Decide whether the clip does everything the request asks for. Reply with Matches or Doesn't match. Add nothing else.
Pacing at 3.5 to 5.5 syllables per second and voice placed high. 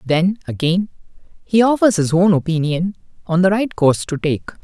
Doesn't match